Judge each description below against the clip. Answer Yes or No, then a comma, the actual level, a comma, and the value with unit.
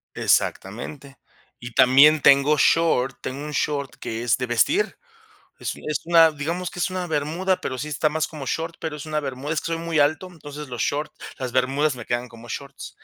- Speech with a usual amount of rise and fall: Yes, average, 3.6 semitones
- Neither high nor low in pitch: Yes, medium, 145 Hz